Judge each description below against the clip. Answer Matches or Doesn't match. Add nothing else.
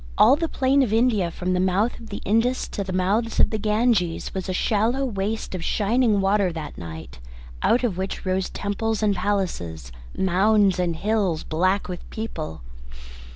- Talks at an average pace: Matches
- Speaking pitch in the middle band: Doesn't match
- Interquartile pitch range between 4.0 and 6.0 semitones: Doesn't match